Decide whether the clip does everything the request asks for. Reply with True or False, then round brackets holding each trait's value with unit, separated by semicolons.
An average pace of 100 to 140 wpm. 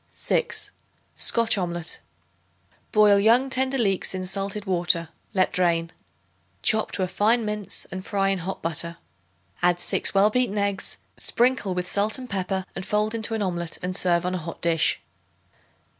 False (160 wpm)